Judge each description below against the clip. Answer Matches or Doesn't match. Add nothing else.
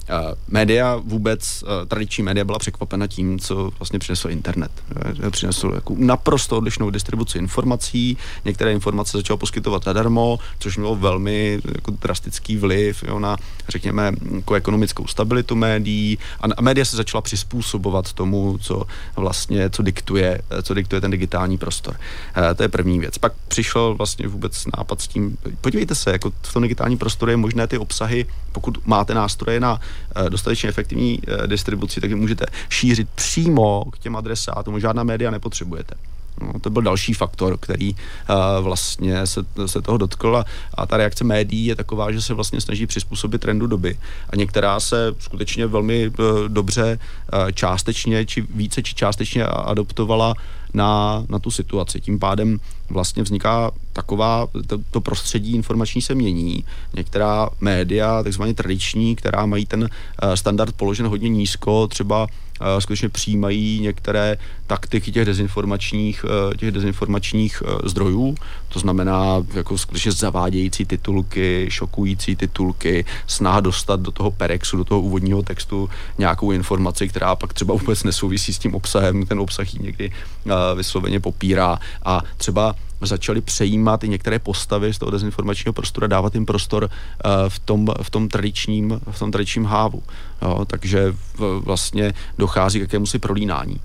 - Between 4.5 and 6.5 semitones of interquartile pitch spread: Doesn't match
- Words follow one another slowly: Doesn't match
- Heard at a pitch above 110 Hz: Doesn't match